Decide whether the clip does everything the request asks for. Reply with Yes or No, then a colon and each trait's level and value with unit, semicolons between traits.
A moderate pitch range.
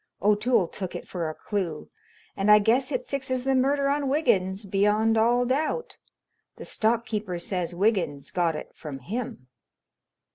No: wide, 5.8 semitones